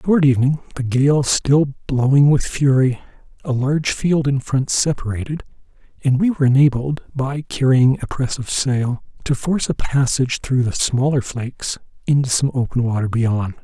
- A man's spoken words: Yes, male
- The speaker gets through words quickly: No, average, 165 wpm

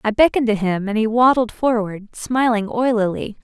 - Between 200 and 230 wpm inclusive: No, average, 175 wpm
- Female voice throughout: Yes, female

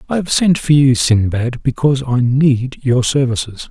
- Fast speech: No, average, 180 wpm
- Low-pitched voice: Yes, low, 130 Hz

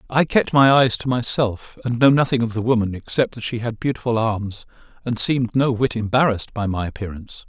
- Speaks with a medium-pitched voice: No, low, 120 Hz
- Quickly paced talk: Yes, fast, 210 wpm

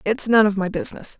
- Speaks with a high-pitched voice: Yes, high, 210 Hz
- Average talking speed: No, fast, 250 wpm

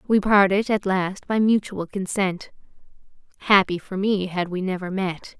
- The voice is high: Yes, high, 195 Hz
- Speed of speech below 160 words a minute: Yes, average, 145 wpm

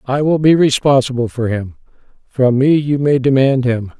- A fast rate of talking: No, average, 180 wpm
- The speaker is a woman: No, male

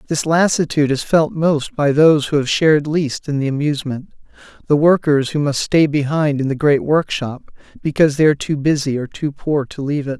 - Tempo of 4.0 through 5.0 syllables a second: No, 5.6 syllables/s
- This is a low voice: No, medium, 145 Hz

